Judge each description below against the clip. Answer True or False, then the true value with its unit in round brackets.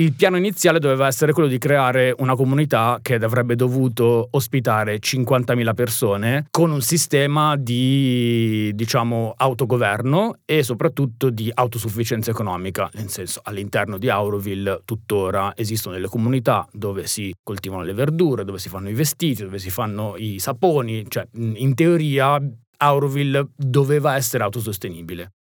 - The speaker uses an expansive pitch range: False (4.6 semitones)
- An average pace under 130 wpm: False (135 wpm)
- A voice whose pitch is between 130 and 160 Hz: False (120 Hz)